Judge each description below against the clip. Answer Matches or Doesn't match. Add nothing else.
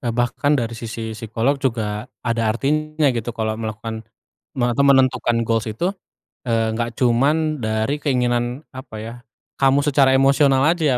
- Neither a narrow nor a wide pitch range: Matches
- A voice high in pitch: Doesn't match